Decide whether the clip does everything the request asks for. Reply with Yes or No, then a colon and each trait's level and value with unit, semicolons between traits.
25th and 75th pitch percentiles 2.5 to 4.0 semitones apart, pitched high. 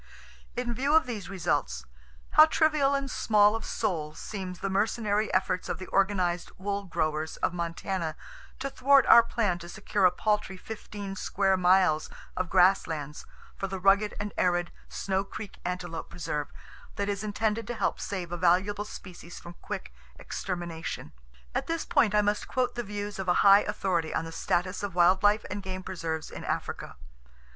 Yes: average, 3.0 semitones; high, 195 Hz